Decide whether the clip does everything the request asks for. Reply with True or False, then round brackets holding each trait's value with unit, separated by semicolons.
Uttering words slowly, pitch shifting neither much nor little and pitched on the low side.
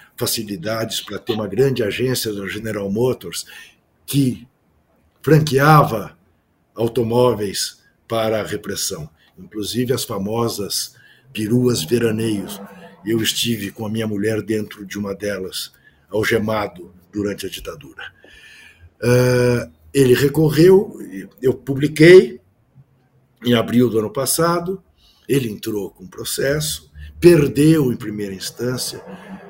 True (105 wpm; 4.1 semitones; 115 Hz)